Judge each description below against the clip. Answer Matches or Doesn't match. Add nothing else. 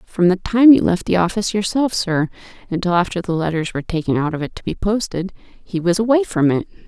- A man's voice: Doesn't match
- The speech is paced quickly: Matches